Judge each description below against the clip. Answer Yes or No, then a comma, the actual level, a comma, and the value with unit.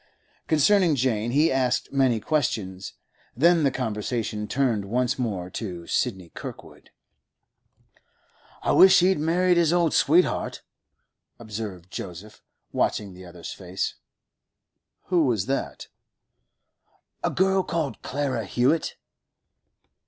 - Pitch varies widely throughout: Yes, wide, 7.1 semitones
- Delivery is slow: Yes, slow, 110 wpm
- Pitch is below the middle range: Yes, low, 125 Hz